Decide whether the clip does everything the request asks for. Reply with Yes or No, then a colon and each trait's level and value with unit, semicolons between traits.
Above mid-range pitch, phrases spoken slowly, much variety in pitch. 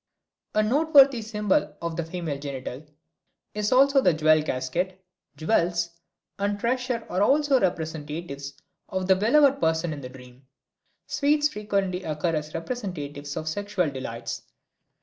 No: medium, 175 Hz; slow, 130 wpm; wide, 6.3 semitones